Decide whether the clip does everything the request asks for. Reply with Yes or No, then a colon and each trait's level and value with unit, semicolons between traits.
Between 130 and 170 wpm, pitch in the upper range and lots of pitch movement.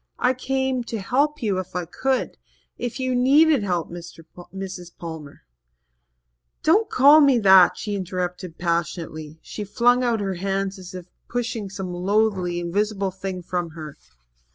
Yes: average, 150 wpm; high, 195 Hz; wide, 5.7 semitones